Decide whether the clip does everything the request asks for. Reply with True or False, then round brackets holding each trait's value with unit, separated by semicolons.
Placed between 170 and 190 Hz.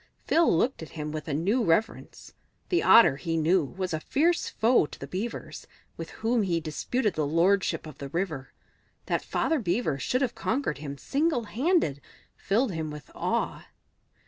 True (185 Hz)